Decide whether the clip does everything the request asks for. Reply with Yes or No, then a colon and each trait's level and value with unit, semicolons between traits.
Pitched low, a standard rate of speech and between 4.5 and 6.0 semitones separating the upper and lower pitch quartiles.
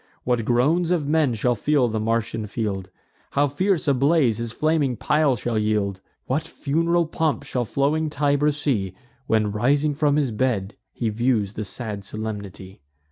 Yes: low, 125 Hz; average, 160 wpm; wide, 5.5 semitones